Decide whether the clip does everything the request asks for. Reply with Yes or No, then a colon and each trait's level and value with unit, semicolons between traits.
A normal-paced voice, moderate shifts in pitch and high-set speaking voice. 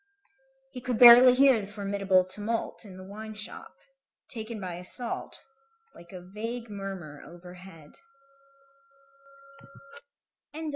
No: slow, 105 wpm; average, 3.8 semitones; high, 200 Hz